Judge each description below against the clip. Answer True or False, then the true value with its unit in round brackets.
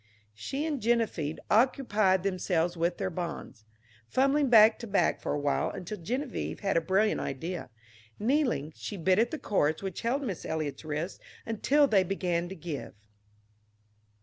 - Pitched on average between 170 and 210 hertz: True (190 Hz)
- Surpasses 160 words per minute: False (155 wpm)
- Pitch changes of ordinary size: False (5.7 semitones)